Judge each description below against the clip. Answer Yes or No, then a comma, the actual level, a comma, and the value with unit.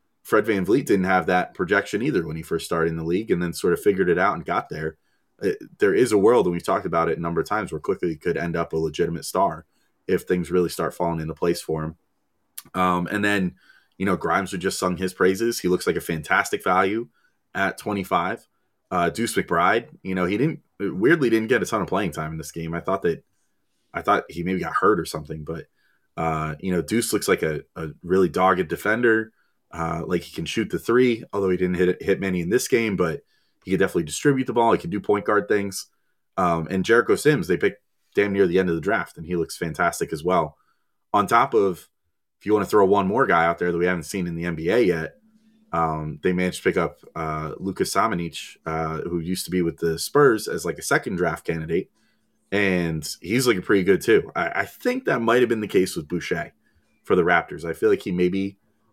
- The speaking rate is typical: No, fast, 240 wpm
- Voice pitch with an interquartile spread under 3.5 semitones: Yes, average, 3.1 semitones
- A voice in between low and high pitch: No, very low, 90 Hz